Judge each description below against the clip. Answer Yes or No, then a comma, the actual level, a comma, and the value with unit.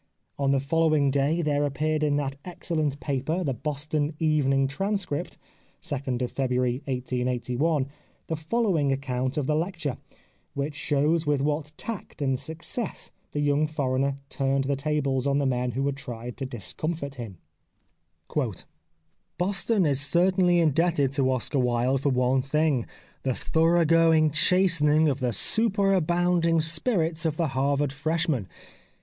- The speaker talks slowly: No, average, 145 wpm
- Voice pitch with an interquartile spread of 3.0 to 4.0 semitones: Yes, average, 3.3 semitones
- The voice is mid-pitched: Yes, medium, 145 Hz